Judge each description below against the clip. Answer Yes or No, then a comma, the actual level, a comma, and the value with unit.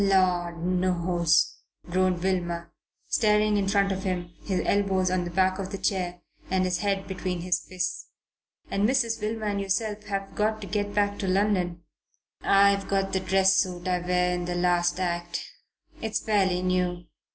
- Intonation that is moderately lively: No, narrow, 2.0 semitones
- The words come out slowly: No, average, 170 wpm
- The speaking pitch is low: No, medium, 185 Hz